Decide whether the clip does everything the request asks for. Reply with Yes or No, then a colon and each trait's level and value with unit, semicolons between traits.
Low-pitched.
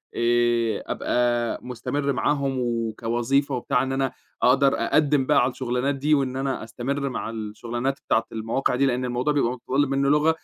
Yes: low, 130 Hz